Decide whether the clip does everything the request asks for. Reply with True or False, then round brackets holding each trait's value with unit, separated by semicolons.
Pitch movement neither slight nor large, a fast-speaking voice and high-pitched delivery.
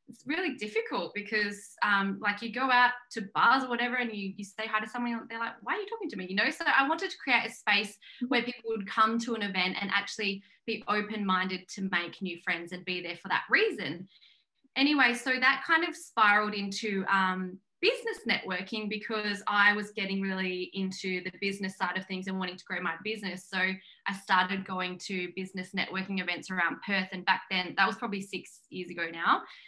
True (3.6 semitones; 215 wpm; 205 Hz)